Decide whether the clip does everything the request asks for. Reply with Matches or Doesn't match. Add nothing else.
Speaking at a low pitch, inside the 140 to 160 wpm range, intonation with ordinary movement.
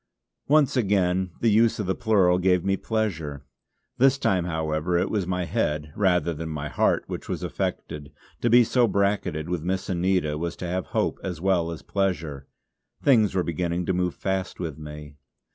Doesn't match